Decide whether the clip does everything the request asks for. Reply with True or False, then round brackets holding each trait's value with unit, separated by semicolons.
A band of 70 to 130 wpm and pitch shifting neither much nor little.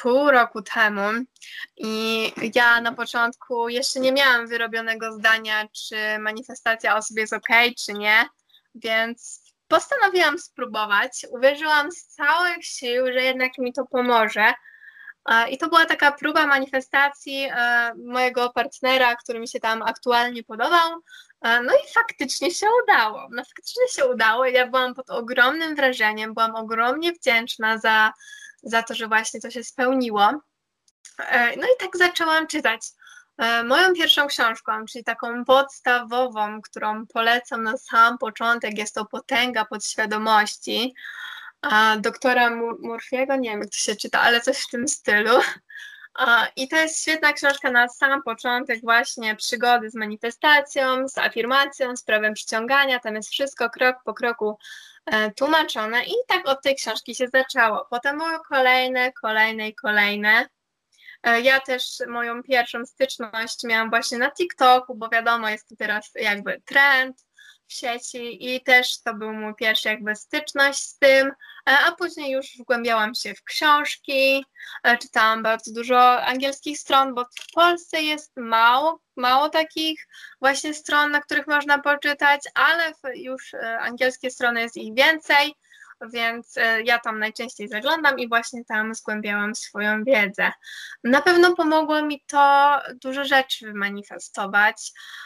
False (140 wpm; 3.8 semitones)